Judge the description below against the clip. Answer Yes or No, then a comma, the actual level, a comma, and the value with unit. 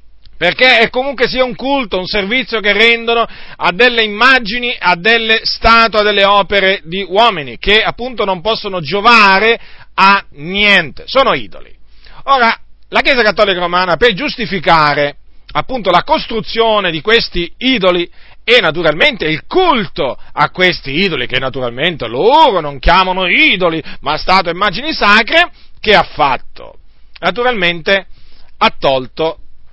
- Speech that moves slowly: No, average, 135 wpm